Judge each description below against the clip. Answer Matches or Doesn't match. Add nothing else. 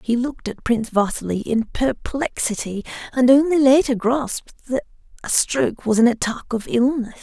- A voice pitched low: Doesn't match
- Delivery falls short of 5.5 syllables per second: Matches